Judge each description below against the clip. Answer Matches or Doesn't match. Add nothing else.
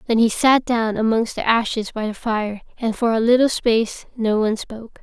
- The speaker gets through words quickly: Matches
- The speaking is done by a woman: Matches